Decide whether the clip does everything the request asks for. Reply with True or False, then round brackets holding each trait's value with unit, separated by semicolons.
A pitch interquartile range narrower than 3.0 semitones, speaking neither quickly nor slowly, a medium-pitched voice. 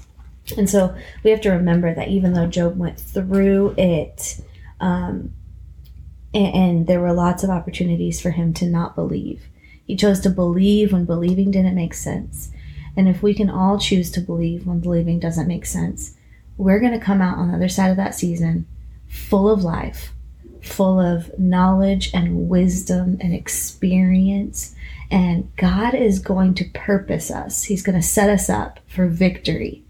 True (2.4 semitones; 170 wpm; 180 Hz)